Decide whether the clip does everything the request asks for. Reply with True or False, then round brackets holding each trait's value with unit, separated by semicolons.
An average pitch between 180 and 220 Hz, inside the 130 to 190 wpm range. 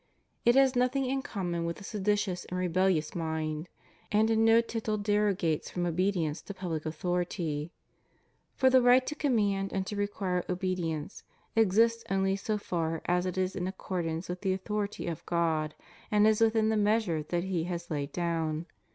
True (185 Hz; 175 wpm)